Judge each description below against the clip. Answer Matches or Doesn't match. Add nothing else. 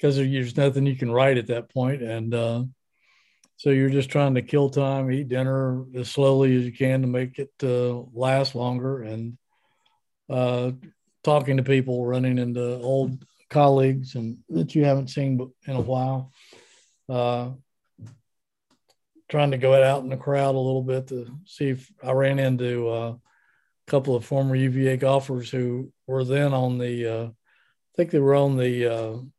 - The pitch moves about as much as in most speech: Doesn't match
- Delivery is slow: Doesn't match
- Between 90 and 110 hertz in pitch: Doesn't match